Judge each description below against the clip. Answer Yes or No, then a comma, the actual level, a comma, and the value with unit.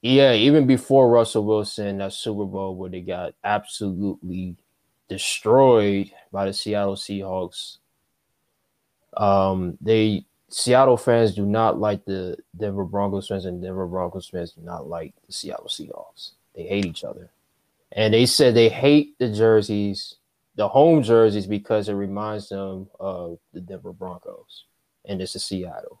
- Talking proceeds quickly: No, average, 150 wpm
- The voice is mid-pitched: No, low, 100 Hz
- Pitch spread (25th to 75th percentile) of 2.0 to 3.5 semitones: Yes, average, 2.7 semitones